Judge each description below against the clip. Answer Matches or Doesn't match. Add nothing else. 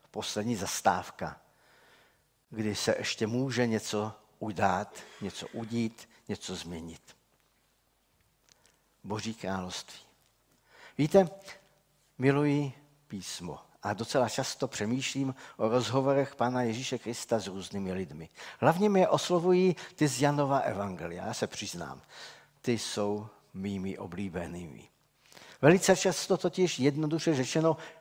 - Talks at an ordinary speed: Doesn't match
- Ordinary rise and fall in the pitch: Doesn't match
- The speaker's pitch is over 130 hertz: Doesn't match